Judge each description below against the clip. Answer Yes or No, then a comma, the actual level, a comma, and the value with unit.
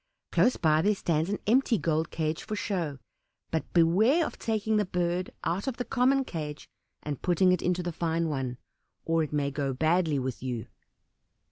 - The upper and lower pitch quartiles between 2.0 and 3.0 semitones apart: No, average, 5.1 semitones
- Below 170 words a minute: No, average, 180 wpm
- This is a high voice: No, medium, 170 Hz